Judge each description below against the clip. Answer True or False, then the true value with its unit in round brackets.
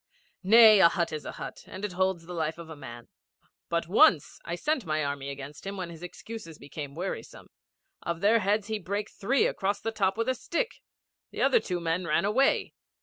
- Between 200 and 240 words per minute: True (205 wpm)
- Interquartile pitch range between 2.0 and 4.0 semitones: False (4.5 semitones)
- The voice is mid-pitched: True (180 Hz)